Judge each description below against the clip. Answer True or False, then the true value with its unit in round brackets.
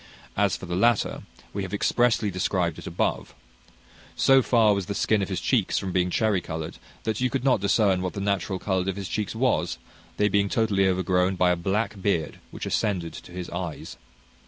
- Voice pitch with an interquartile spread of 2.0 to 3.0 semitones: True (2.7 semitones)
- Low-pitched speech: True (95 Hz)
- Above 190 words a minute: True (200 wpm)